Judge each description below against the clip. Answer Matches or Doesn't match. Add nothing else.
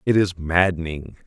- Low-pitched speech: Matches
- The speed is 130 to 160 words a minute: Matches